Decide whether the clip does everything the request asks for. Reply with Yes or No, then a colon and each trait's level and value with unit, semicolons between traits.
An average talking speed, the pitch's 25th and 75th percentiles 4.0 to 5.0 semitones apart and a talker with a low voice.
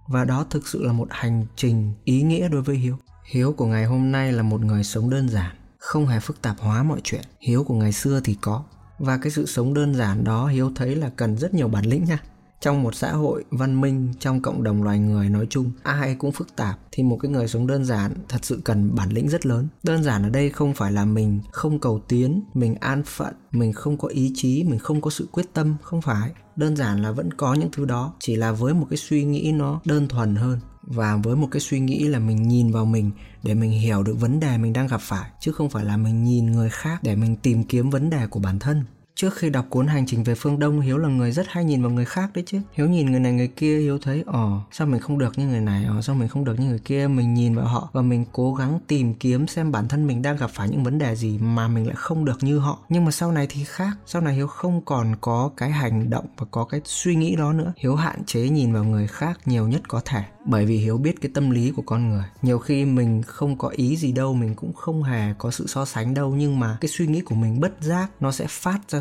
No: fast, 275 wpm; average, 4.4 semitones; low, 130 Hz